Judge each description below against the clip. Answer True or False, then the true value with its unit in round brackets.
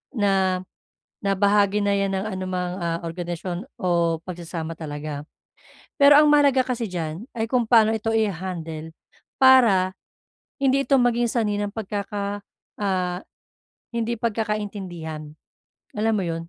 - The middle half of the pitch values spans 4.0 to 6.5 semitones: True (4.3 semitones)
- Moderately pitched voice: False (200 Hz)